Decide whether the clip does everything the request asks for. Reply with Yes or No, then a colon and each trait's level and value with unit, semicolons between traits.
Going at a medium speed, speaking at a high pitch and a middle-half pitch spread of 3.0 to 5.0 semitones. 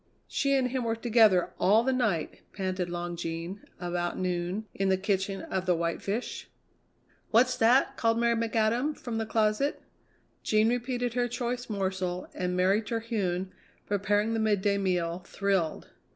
Yes: average, 150 wpm; high, 205 Hz; average, 3.9 semitones